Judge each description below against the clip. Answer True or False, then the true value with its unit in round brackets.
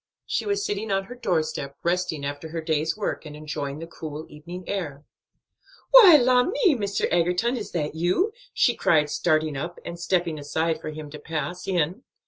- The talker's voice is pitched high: False (170 Hz)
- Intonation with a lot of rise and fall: False (4.5 semitones)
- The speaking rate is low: False (180 wpm)